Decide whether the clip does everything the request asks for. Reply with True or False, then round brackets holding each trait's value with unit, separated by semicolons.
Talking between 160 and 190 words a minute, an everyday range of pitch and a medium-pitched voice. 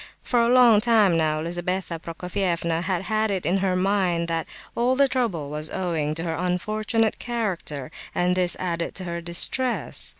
True (170 wpm; 4.3 semitones; 180 Hz)